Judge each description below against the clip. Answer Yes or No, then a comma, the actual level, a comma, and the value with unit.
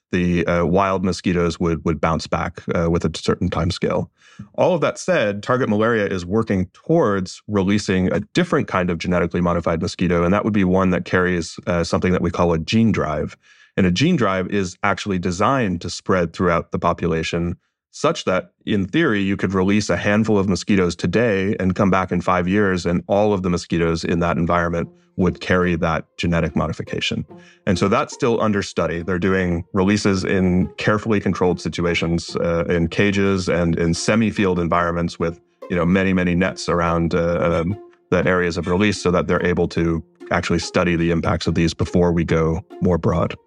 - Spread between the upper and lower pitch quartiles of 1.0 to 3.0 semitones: Yes, narrow, 2.6 semitones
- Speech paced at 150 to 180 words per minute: No, average, 190 wpm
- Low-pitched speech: Yes, very low, 90 Hz